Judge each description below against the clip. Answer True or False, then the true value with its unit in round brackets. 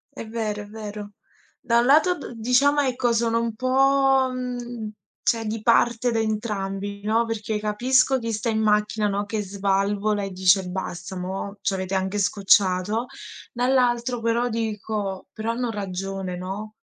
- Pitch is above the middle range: True (215 Hz)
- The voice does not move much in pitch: False (3.1 semitones)